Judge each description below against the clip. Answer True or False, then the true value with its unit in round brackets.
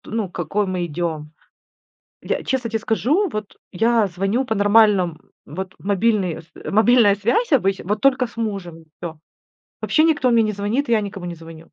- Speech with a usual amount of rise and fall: True (4.4 semitones)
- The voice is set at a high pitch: True (205 Hz)